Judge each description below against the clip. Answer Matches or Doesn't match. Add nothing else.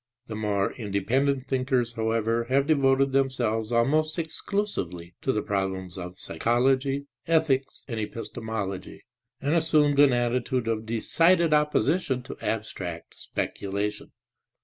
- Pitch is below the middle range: Matches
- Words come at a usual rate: Doesn't match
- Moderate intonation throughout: Matches